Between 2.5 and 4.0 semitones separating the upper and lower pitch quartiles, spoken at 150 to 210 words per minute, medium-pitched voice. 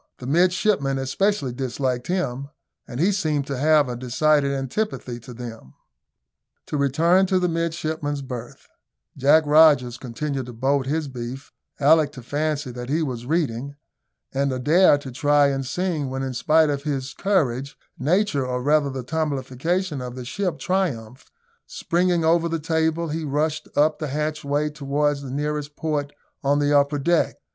Yes: average, 3.3 semitones; average, 160 wpm; medium, 145 Hz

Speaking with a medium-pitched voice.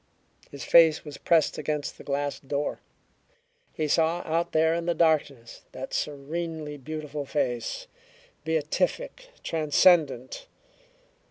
Yes: medium, 155 Hz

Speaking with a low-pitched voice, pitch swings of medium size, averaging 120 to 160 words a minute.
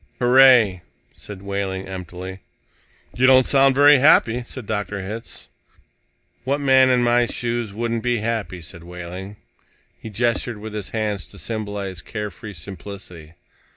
Yes: low, 105 Hz; average, 4.2 semitones; average, 140 wpm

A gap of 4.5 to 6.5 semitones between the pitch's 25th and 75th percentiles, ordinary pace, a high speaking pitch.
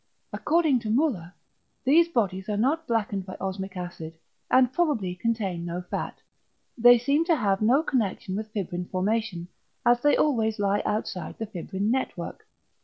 Yes: average, 5.1 semitones; average, 155 wpm; high, 215 Hz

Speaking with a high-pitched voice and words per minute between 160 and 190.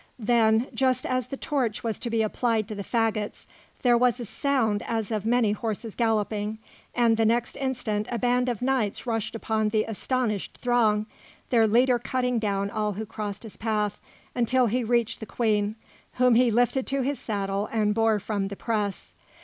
Yes: high, 225 Hz; average, 185 wpm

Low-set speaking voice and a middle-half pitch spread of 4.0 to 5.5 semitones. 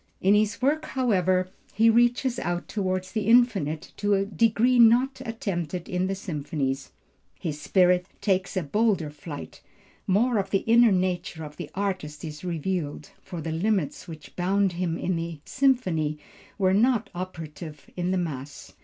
No: medium, 185 Hz; average, 4.9 semitones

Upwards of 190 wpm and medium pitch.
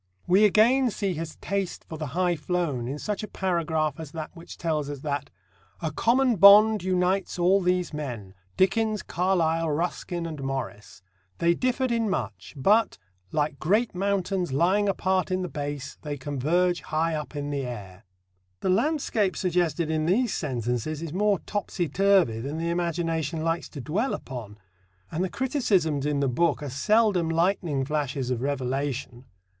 No: average, 160 wpm; medium, 165 Hz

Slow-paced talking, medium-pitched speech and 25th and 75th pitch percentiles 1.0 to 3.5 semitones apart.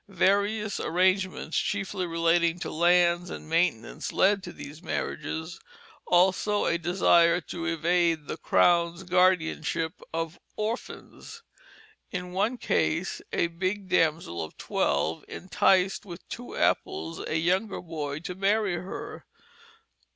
Yes: slow, 120 wpm; medium, 175 Hz; narrow, 2.4 semitones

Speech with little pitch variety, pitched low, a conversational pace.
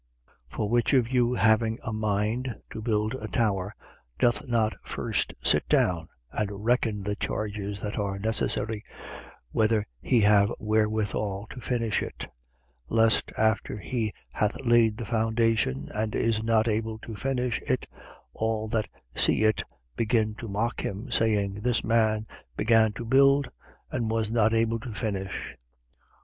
Yes: narrow, 1.6 semitones; low, 110 Hz; average, 155 wpm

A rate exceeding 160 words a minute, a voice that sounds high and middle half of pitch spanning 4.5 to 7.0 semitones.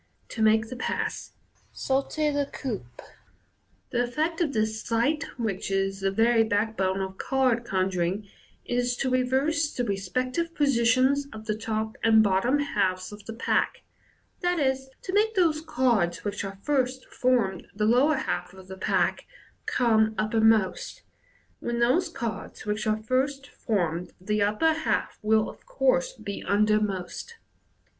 No: average, 150 wpm; high, 225 Hz; average, 4.8 semitones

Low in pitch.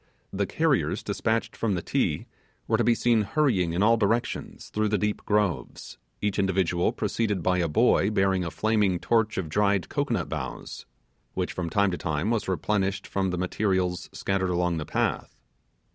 Yes: very low, 95 Hz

